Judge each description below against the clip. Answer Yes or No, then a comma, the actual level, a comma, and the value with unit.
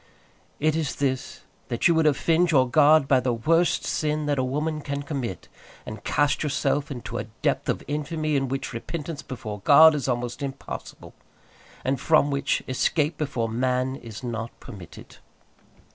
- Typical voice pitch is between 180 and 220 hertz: No, medium, 140 Hz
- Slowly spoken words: No, average, 160 wpm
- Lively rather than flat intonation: No, average, 3.3 semitones